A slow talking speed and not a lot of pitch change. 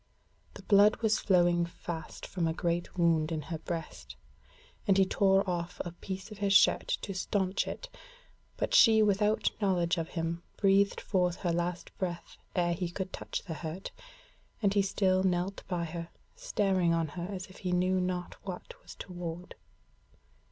No: average, 170 wpm; narrow, 2.2 semitones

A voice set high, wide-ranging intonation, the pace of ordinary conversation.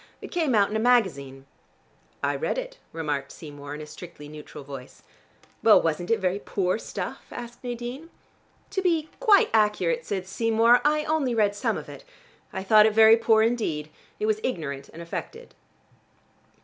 Yes: high, 215 Hz; wide, 7.1 semitones; average, 170 wpm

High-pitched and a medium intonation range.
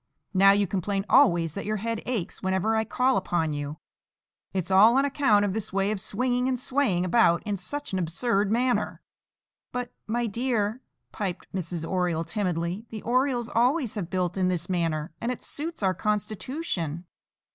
Yes: high, 205 Hz; average, 5.0 semitones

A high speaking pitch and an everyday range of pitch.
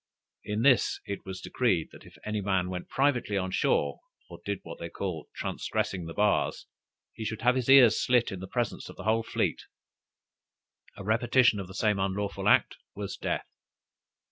No: low, 105 Hz; average, 3.6 semitones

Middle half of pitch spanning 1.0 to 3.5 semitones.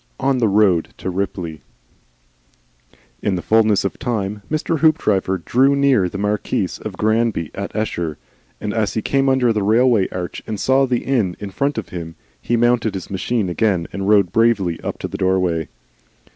No: average, 4.3 semitones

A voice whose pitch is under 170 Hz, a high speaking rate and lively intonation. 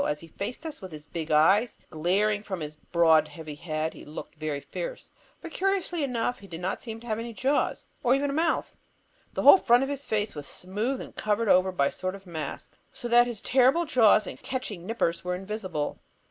No: high, 205 Hz; fast, 215 wpm; wide, 6.9 semitones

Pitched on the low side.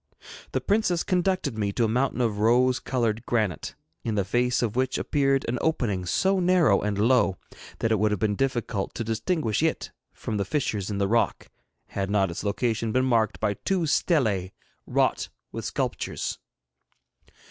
Yes: low, 115 Hz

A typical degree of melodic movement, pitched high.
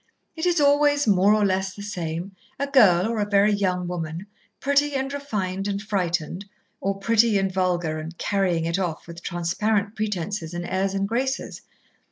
Yes: average, 3.7 semitones; high, 195 Hz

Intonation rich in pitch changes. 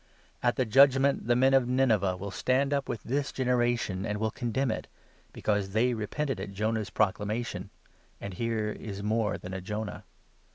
No: average, 3.8 semitones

